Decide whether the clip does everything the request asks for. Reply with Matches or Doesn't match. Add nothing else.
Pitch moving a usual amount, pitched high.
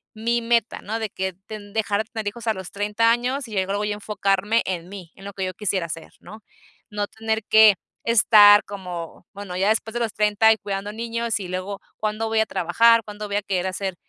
Doesn't match